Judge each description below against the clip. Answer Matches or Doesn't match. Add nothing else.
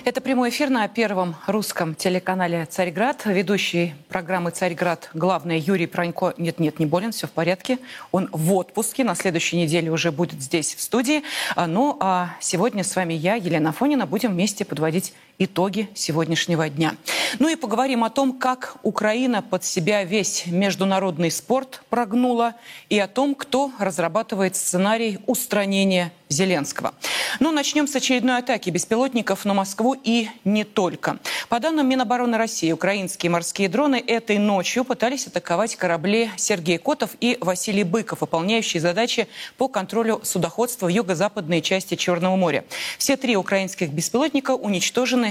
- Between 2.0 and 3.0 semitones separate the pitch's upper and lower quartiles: Doesn't match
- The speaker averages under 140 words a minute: Doesn't match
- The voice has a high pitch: Matches